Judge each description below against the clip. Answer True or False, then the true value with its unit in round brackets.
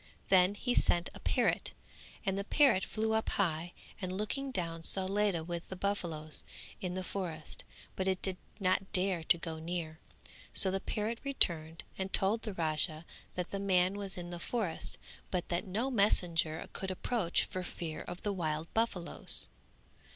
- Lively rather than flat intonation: False (2.8 semitones)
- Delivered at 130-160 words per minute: False (170 wpm)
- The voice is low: False (185 Hz)